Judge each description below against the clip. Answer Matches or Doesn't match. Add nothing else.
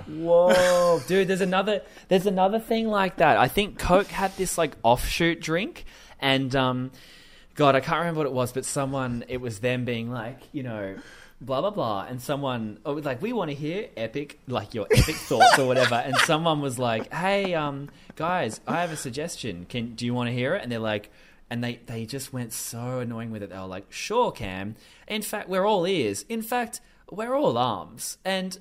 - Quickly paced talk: Matches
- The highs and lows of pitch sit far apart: Matches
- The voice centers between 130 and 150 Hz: Matches